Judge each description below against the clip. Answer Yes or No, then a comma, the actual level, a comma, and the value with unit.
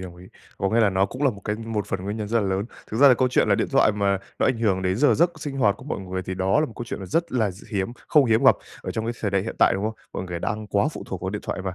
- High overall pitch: No, low, 105 Hz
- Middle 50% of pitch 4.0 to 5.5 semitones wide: No, average, 3.5 semitones